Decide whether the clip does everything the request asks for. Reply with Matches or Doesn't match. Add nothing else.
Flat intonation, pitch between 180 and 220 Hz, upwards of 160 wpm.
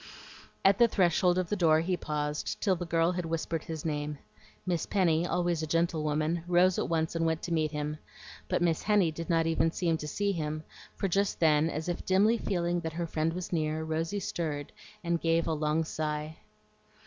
Doesn't match